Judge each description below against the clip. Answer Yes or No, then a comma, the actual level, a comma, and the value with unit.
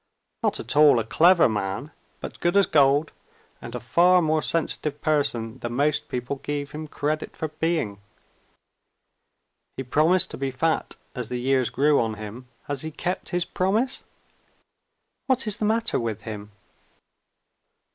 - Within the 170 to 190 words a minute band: No, average, 150 wpm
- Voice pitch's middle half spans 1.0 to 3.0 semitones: No, average, 5.2 semitones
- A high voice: No, medium, 145 Hz